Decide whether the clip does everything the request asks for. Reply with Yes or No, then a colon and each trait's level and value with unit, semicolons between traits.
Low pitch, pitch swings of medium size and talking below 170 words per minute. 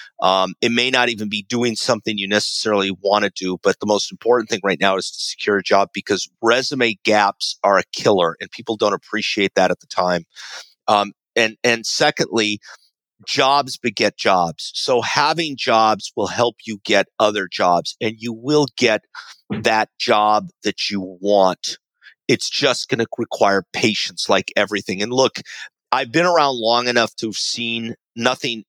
No: low, 115 Hz; average, 3.0 semitones; average, 175 wpm